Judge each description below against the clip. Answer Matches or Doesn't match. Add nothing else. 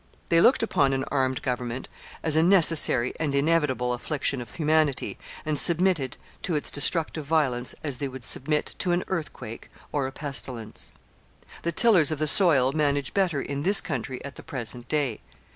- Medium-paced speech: Matches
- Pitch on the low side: Doesn't match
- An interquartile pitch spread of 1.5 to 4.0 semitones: Matches